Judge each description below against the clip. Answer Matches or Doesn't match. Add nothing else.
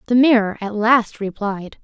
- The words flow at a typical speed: Matches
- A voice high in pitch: Matches